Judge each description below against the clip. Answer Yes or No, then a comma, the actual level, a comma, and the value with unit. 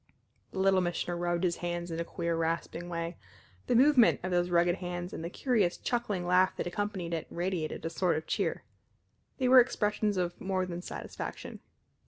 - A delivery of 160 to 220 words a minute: Yes, average, 185 wpm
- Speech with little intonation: Yes, narrow, 2.1 semitones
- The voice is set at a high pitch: No, medium, 175 Hz